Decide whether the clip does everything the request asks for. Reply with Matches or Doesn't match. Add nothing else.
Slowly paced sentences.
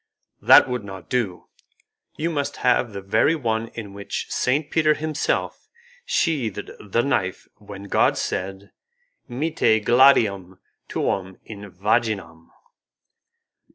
Matches